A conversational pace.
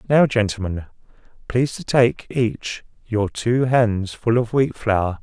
Yes: average, 150 wpm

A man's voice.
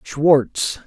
Yes: male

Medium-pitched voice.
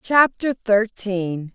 No: high, 215 Hz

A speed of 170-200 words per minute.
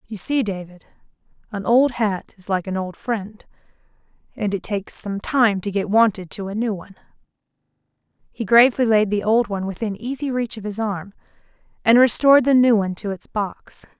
Yes: average, 185 wpm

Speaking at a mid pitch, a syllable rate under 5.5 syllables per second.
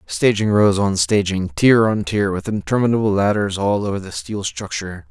No: low, 100 Hz; 5.0 syllables/s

